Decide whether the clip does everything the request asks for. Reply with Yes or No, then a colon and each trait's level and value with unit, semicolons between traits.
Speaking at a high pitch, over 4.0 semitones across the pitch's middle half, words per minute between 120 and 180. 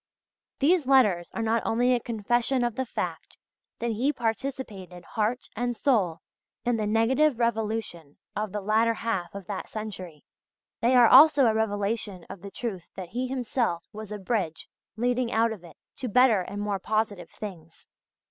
No: high, 220 Hz; average, 3.5 semitones; average, 165 wpm